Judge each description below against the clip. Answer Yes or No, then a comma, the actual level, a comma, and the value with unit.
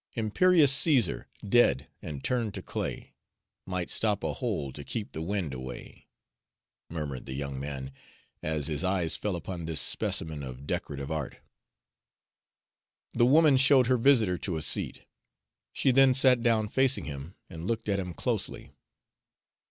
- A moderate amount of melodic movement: No, wide, 8.6 semitones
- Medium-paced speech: Yes, average, 150 wpm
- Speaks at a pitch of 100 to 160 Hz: No, very low, 90 Hz